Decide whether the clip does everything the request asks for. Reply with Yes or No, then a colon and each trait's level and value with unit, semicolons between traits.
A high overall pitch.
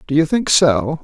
No: medium, 150 Hz